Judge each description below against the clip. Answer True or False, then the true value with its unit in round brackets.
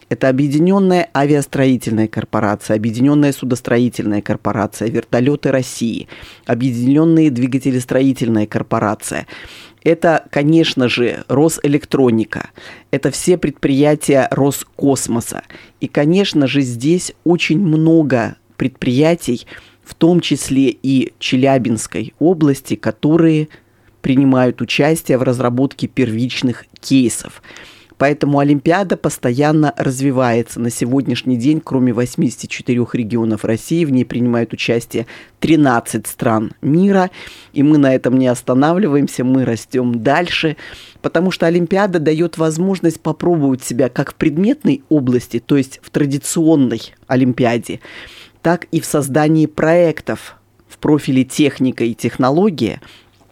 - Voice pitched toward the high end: False (135 Hz)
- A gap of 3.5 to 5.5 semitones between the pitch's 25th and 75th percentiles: True (4.5 semitones)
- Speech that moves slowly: True (105 wpm)